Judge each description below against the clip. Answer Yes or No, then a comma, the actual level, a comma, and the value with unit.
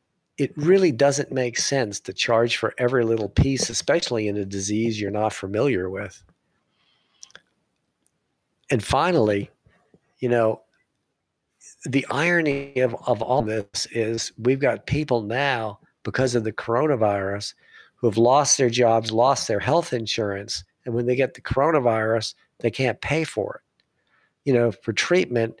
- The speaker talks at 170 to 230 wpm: No, average, 145 wpm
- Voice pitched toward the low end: Yes, low, 120 Hz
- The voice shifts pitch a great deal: No, average, 3.9 semitones